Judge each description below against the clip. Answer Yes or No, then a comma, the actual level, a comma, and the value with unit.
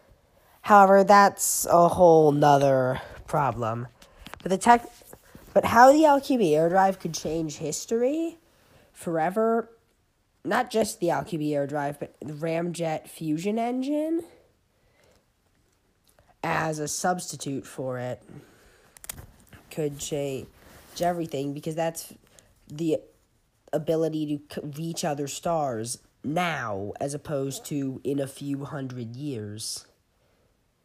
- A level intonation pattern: No, average, 4.5 semitones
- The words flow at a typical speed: No, slow, 105 wpm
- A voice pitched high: No, medium, 155 Hz